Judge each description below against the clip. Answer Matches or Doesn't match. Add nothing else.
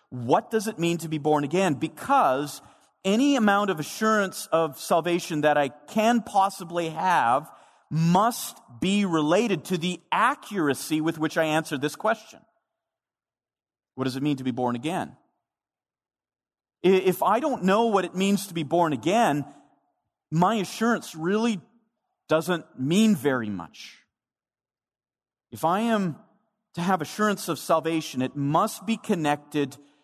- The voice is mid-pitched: Matches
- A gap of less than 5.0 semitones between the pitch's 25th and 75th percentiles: Doesn't match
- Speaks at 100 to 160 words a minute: Matches